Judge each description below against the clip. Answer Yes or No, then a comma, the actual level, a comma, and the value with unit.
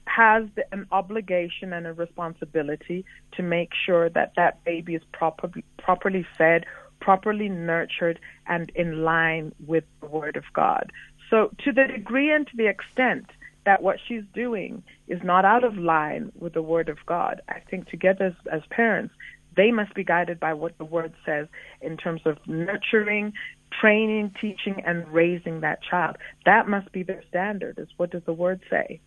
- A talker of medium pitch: Yes, medium, 180 Hz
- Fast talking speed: No, average, 170 wpm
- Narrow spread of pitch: No, average, 4.0 semitones